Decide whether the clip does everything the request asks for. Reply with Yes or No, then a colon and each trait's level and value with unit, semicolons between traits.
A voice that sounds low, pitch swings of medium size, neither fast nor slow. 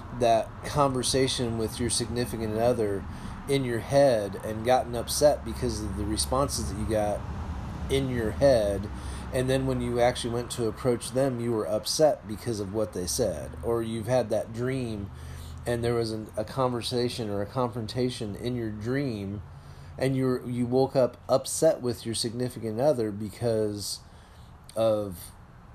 Yes: low, 115 Hz; average, 3.1 semitones; average, 160 wpm